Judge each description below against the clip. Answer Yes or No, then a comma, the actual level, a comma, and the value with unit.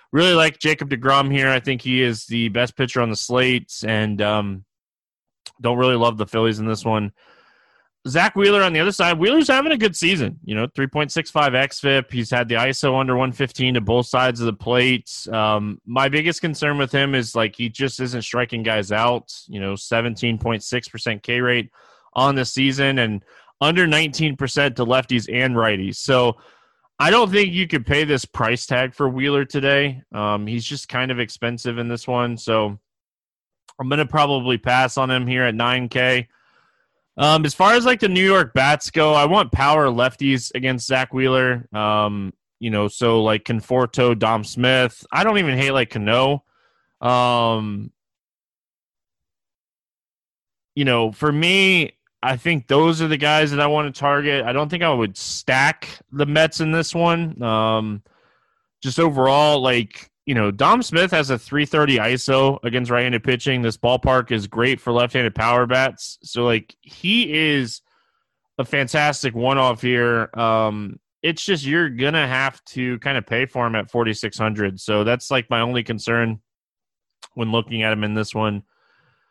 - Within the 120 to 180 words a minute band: Yes, average, 175 wpm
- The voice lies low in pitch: Yes, low, 125 Hz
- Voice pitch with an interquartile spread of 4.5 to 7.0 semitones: No, average, 3.7 semitones